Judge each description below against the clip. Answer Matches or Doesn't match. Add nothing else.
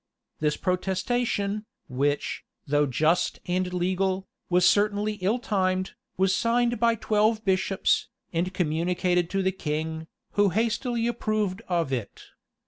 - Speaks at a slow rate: Matches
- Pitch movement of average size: Matches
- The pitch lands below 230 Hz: Matches